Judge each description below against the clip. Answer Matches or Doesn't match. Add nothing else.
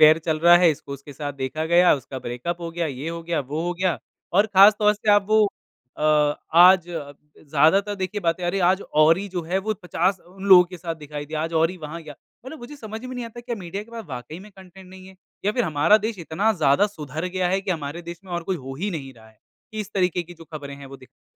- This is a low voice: Doesn't match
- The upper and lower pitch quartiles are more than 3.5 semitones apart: Matches